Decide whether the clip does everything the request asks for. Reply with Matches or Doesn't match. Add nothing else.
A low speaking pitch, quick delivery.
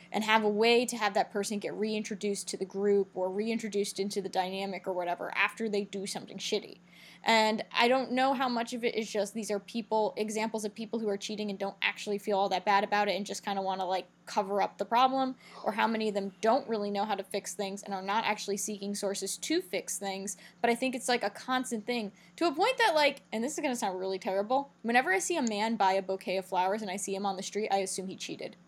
Doesn't match